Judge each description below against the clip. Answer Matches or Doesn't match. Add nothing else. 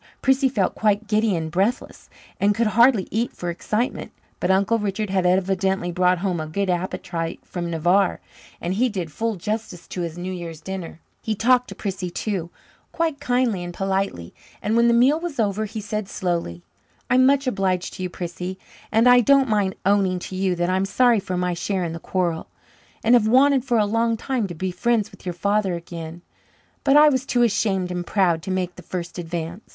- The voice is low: Doesn't match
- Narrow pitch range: Doesn't match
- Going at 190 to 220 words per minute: Matches